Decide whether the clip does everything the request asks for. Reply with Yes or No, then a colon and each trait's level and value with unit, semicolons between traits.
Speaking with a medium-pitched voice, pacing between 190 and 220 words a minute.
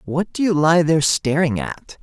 Yes: medium, 155 Hz; fast, 205 wpm